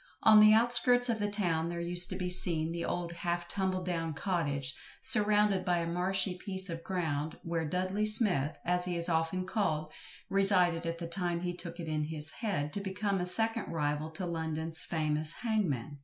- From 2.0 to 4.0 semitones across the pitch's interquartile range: Yes, average, 3.2 semitones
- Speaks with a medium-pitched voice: Yes, medium, 175 Hz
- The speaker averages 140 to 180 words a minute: No, average, 190 wpm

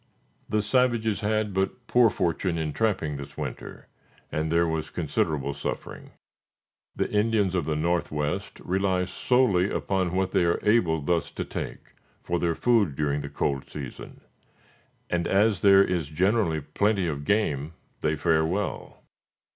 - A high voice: No, very low, 90 Hz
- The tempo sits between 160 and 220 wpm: No, average, 145 wpm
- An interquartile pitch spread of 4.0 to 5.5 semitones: Yes, average, 4.9 semitones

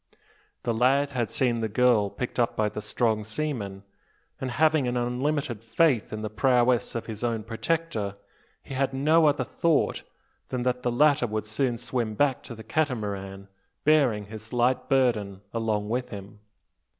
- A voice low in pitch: Yes, low, 120 Hz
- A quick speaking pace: No, average, 165 wpm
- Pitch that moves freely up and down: No, average, 3.6 semitones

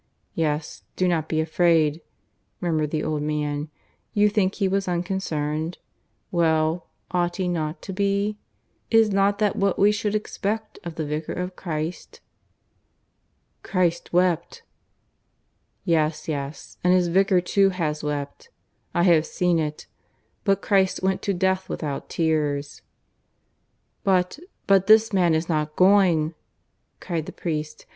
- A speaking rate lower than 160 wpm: Yes, slow, 135 wpm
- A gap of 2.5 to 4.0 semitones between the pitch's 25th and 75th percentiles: Yes, average, 3.7 semitones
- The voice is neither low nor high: Yes, medium, 175 Hz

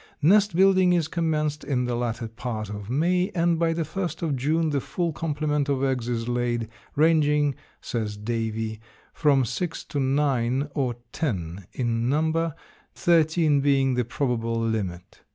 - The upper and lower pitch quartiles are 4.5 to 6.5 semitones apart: Yes, average, 5.2 semitones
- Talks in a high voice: No, medium, 140 Hz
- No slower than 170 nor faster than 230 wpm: No, average, 155 wpm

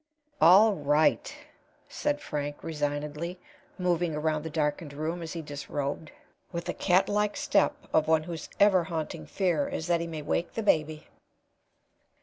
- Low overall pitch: No, medium, 160 Hz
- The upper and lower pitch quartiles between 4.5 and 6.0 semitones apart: No, average, 2.9 semitones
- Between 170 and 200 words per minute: No, average, 150 wpm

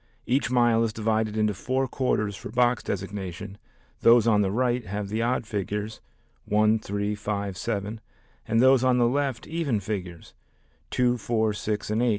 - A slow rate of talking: No, average, 165 wpm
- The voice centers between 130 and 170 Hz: No, low, 110 Hz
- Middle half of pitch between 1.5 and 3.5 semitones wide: Yes, average, 2.8 semitones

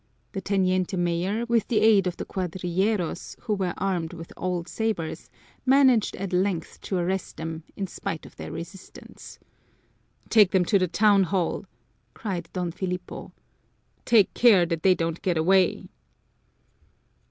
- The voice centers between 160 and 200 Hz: Yes, medium, 185 Hz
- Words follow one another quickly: No, average, 145 wpm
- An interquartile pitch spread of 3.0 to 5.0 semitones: No, narrow, 2.6 semitones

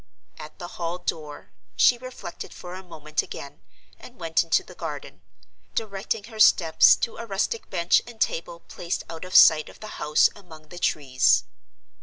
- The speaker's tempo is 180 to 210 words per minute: No, average, 170 wpm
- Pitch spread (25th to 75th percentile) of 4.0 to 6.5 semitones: Yes, average, 4.3 semitones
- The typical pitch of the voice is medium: Yes, medium, 175 Hz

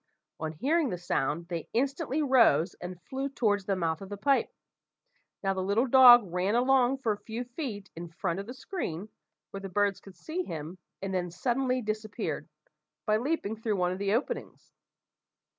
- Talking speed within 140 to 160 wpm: No, average, 180 wpm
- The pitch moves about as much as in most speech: No, wide, 5.7 semitones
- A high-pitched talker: Yes, high, 210 Hz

